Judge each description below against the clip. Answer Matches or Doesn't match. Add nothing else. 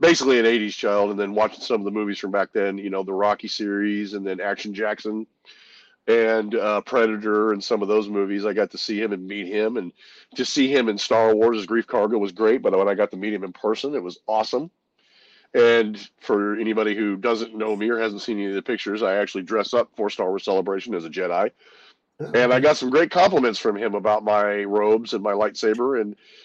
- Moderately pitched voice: Doesn't match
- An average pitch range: Doesn't match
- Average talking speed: Doesn't match